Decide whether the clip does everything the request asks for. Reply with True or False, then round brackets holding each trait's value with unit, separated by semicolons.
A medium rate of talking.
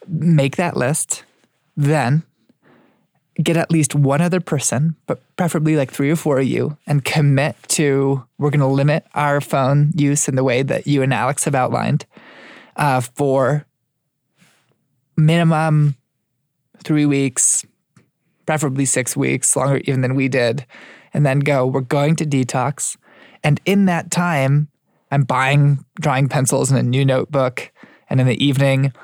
True (150 wpm)